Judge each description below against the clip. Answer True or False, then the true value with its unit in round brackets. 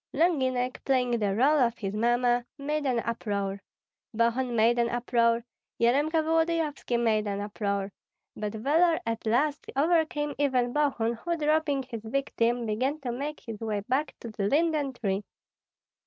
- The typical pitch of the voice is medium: False (245 Hz)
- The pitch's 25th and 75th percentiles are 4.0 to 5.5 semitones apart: True (4.4 semitones)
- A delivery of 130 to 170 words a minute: True (150 wpm)